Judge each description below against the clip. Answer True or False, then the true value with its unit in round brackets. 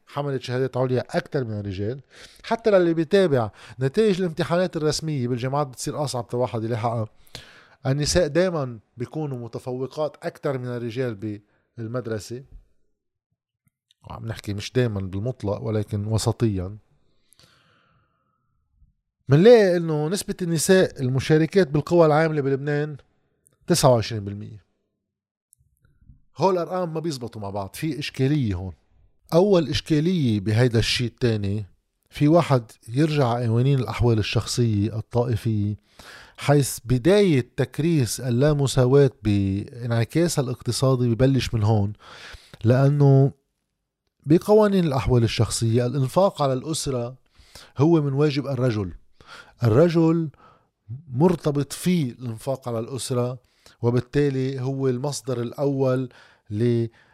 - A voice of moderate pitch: False (130 Hz)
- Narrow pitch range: False (4.8 semitones)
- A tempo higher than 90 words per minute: True (100 wpm)